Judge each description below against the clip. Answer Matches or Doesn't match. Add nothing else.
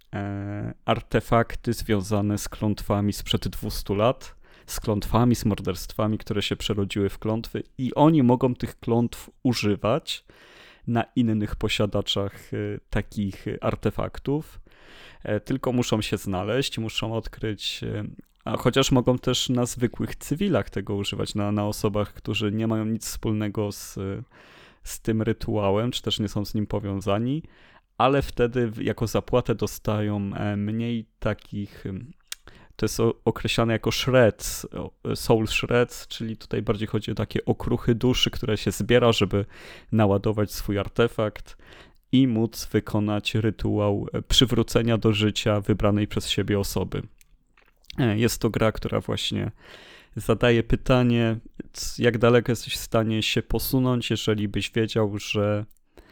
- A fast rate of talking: Doesn't match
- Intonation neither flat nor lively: Doesn't match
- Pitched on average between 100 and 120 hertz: Matches